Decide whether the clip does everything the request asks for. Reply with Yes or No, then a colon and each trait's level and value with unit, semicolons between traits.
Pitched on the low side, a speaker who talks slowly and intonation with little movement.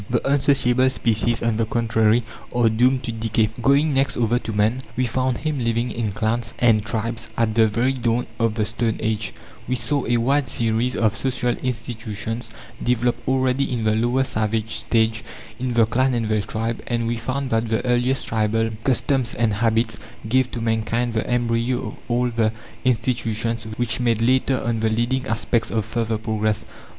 No: low, 115 Hz; average, 180 wpm; narrow, 1.9 semitones